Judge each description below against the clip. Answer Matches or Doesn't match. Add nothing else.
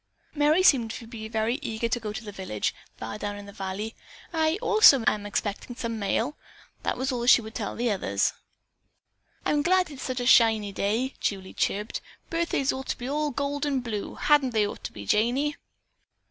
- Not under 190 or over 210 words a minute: Matches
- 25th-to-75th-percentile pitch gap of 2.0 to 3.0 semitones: Doesn't match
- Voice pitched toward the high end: Matches